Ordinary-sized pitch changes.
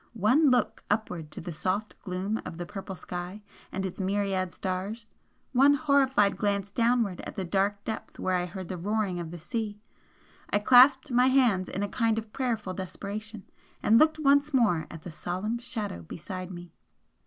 Yes: average, 4.1 semitones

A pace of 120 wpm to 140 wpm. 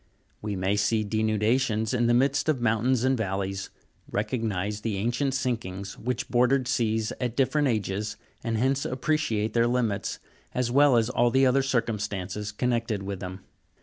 No: average, 150 wpm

